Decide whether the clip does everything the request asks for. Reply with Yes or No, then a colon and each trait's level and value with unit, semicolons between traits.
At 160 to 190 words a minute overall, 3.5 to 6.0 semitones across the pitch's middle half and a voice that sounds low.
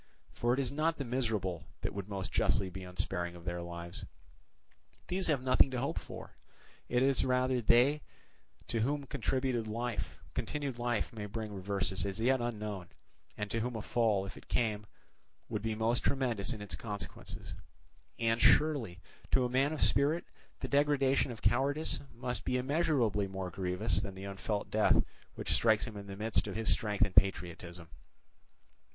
Yes: average, 170 wpm; average, 4.7 semitones; low, 115 Hz